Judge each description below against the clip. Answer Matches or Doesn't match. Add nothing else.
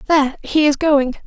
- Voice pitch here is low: Doesn't match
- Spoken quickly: Doesn't match